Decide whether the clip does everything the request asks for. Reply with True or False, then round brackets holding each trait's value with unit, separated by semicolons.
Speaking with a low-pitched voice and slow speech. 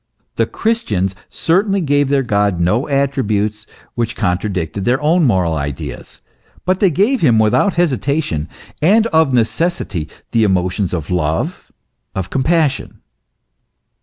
True (120 Hz; 125 wpm)